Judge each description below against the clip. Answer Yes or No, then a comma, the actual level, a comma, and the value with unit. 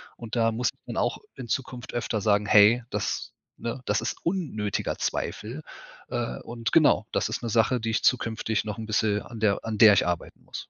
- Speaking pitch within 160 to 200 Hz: No, low, 110 Hz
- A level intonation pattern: Yes, narrow, 2.2 semitones